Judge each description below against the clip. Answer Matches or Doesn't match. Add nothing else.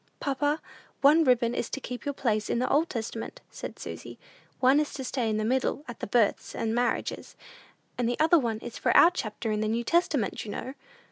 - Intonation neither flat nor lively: Matches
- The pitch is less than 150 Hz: Doesn't match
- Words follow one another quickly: Matches